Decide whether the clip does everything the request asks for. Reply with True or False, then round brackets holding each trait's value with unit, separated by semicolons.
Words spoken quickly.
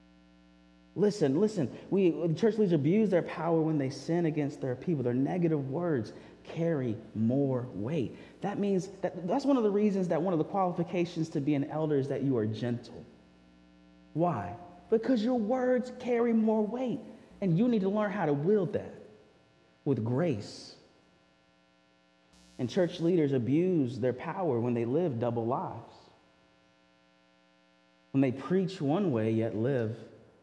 False (155 wpm)